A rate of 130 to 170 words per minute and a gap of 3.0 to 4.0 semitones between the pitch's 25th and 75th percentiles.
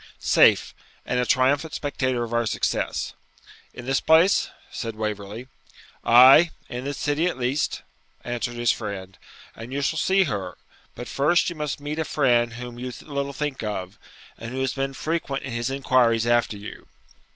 Yes: average, 165 wpm; average, 3.4 semitones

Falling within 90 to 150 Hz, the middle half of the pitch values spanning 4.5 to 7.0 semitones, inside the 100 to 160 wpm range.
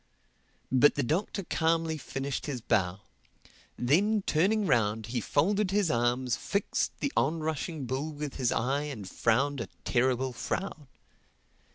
Yes: medium, 140 Hz; average, 5.2 semitones; average, 140 wpm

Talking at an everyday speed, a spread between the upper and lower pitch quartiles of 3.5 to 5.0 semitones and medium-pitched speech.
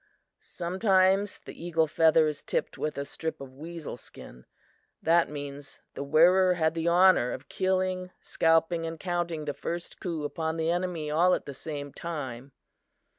No: average, 160 wpm; average, 2.9 semitones; medium, 165 Hz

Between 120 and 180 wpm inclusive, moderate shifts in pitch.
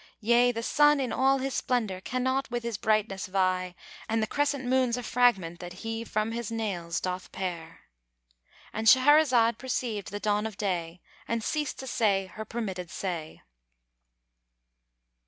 Yes: average, 155 wpm; average, 4.7 semitones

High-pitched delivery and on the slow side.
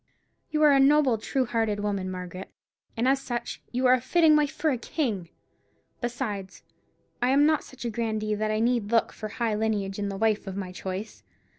No: high, 225 Hz; average, 200 wpm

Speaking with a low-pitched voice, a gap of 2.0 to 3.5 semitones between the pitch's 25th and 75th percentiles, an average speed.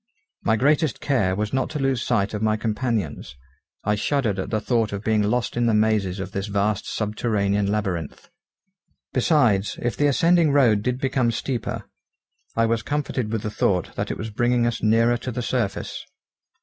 Yes: low, 110 Hz; average, 3.2 semitones; average, 180 wpm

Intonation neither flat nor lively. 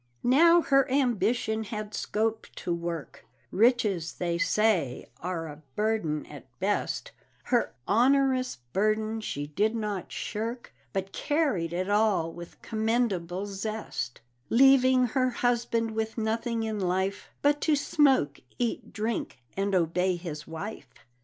Yes: average, 4.9 semitones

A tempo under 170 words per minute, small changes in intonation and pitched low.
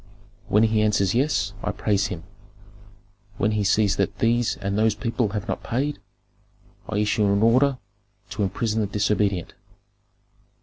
Yes: average, 145 wpm; narrow, 2.2 semitones; low, 105 Hz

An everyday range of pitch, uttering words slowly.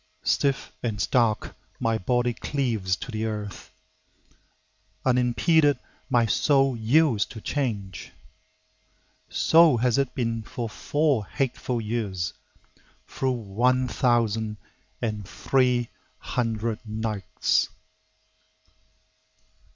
Yes: average, 3.0 semitones; slow, 90 wpm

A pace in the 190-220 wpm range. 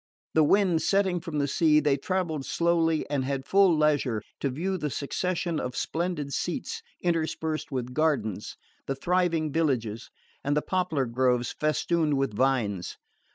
No: average, 150 wpm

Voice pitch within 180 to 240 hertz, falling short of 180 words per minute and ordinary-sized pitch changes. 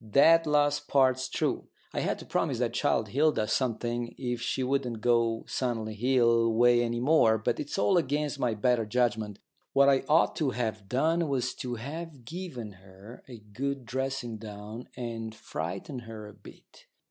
No: low, 120 Hz; average, 170 wpm; average, 3.6 semitones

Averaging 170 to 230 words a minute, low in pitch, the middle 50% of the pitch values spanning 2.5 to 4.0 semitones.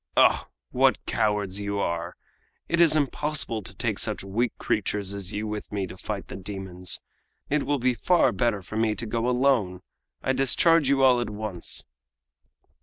No: average, 175 wpm; low, 110 Hz; average, 5.0 semitones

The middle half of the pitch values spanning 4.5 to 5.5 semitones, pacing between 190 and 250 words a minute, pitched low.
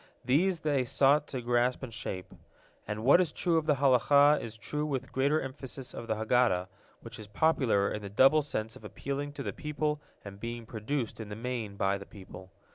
Yes: average, 5.0 semitones; average, 200 wpm; low, 125 Hz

